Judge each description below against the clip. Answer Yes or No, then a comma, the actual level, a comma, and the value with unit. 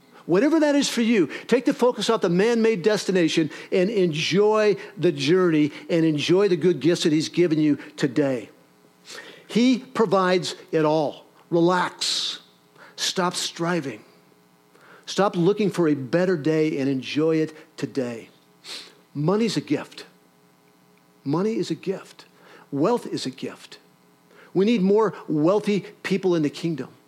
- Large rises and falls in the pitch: Yes, wide, 6.2 semitones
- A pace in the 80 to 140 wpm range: Yes, slow, 135 wpm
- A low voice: No, medium, 170 Hz